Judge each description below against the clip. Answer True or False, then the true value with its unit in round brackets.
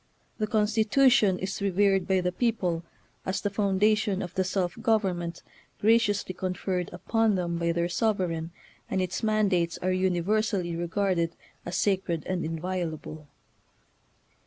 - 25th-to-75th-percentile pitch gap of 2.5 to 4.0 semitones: True (3.1 semitones)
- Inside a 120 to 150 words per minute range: True (135 wpm)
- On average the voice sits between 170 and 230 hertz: True (185 Hz)